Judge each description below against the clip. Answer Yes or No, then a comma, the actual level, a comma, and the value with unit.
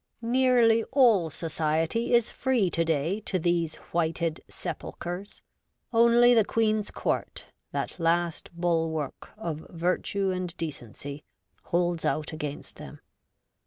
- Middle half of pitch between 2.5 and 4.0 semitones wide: No, average, 5.1 semitones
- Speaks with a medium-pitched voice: Yes, medium, 175 Hz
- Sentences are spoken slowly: Yes, slow, 125 wpm